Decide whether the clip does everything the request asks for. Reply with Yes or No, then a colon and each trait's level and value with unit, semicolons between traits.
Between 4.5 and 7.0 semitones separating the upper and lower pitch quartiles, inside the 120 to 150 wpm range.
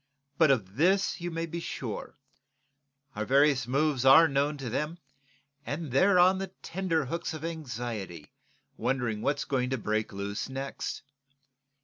Yes: average, 5.3 semitones; average, 140 wpm